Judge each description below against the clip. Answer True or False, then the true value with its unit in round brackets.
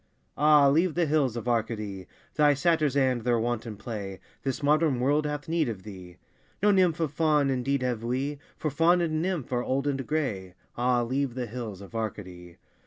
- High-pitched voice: False (130 Hz)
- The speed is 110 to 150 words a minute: False (185 wpm)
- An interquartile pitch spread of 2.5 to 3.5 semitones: False (4.9 semitones)